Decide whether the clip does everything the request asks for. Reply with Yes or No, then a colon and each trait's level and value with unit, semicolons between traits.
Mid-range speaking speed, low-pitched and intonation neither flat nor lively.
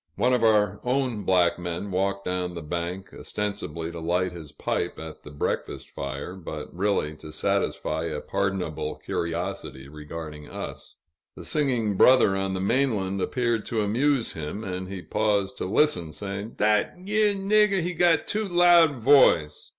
No: average, 160 wpm; very low, 95 Hz; wide, 6.7 semitones